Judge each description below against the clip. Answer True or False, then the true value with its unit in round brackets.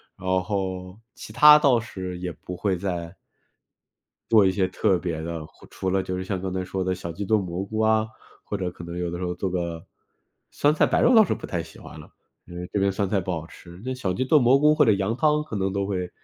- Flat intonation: False (3.4 semitones)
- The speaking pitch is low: True (95 Hz)